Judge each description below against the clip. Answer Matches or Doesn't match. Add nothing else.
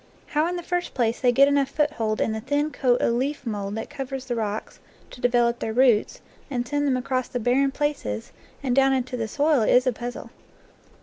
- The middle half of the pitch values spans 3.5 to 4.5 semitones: Doesn't match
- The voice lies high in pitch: Matches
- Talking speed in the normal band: Doesn't match